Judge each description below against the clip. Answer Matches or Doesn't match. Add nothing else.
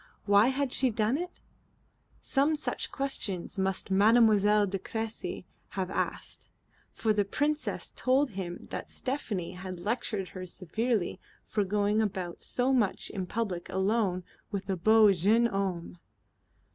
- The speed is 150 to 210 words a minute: Doesn't match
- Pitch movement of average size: Matches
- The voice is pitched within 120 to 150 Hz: Doesn't match